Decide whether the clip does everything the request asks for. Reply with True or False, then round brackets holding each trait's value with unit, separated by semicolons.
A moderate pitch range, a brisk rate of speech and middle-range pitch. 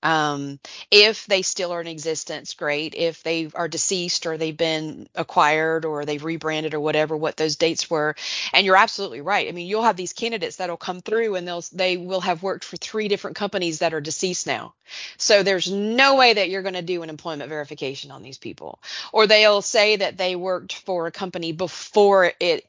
True (3.6 semitones; 210 wpm; 180 Hz)